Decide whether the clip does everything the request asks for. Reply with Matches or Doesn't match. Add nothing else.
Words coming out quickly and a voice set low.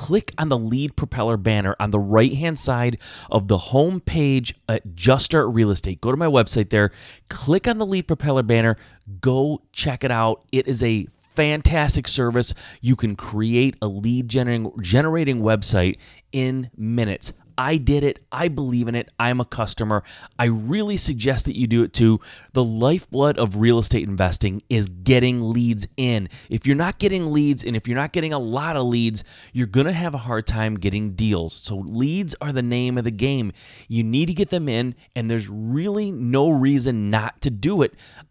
Doesn't match